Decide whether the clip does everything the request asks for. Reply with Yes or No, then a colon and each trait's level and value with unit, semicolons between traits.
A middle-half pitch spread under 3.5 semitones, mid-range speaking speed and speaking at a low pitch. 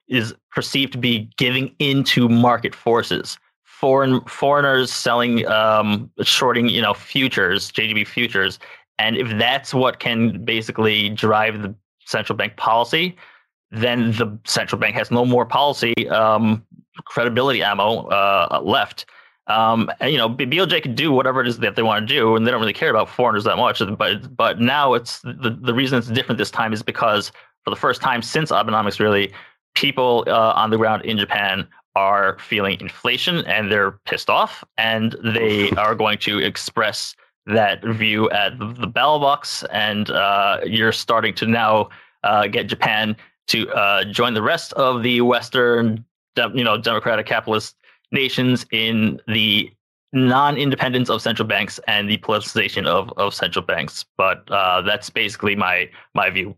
Yes: narrow, 2.6 semitones; average, 165 wpm; low, 115 Hz